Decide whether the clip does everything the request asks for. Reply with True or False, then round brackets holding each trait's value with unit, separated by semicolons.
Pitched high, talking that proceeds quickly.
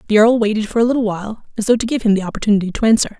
True (215 Hz; 300 wpm)